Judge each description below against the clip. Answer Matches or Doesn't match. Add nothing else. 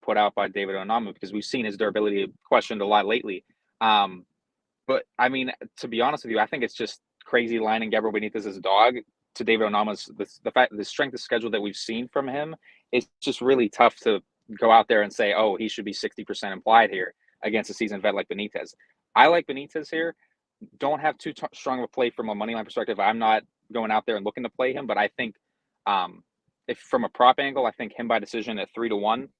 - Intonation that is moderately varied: Matches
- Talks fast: Matches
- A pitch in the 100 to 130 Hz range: Matches